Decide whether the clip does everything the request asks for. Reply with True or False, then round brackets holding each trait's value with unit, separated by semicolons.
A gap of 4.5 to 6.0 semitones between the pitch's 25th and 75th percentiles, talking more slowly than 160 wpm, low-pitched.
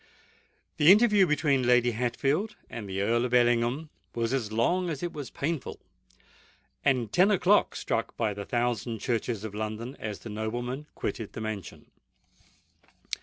True (5.1 semitones; 150 wpm; 120 Hz)